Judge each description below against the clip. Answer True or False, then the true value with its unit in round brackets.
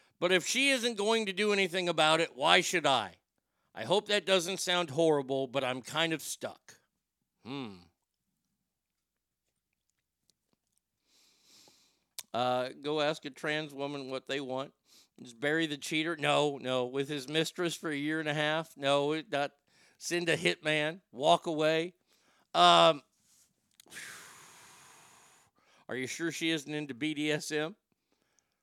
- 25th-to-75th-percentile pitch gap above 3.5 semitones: False (3.2 semitones)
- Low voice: False (155 Hz)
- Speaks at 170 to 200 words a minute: False (135 wpm)